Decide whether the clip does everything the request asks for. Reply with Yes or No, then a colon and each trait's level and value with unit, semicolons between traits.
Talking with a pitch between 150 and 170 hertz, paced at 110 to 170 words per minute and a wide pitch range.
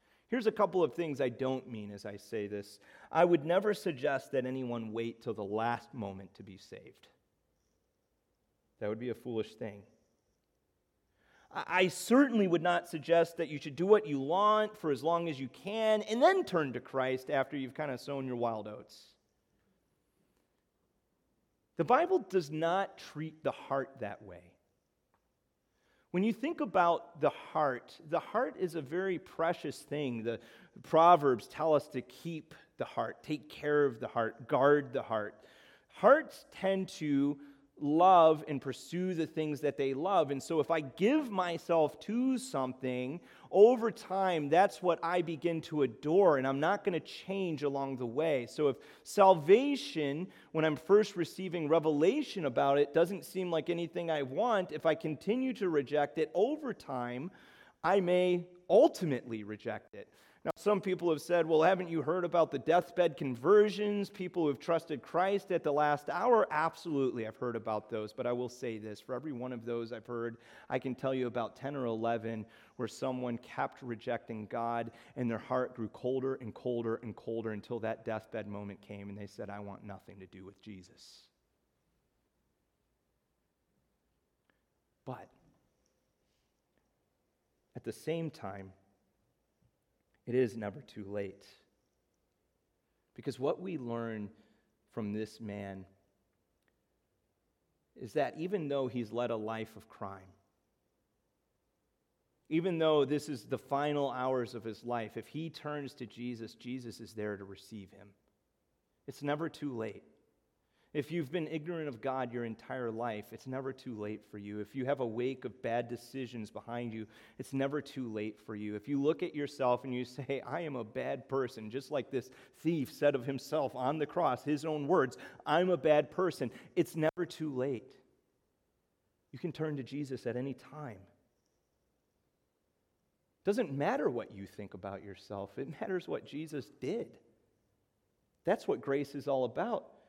No: low, 135 Hz; average, 165 wpm; wide, 6.3 semitones